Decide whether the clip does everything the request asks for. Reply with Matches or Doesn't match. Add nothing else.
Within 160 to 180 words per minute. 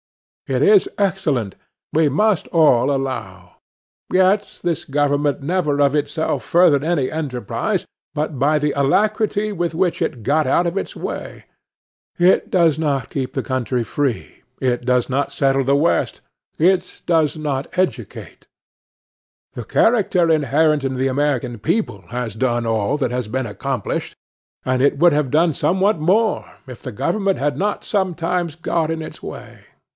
Doesn't match